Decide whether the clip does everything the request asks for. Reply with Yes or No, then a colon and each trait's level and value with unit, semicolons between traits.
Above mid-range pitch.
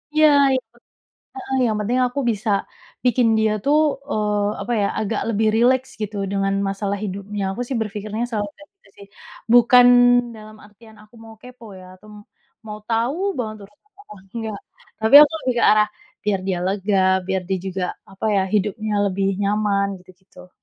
Yes: high, 215 Hz